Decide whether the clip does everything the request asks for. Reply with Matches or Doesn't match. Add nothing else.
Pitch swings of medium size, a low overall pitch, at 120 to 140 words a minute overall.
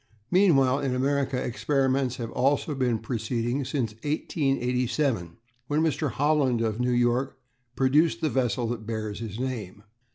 Matches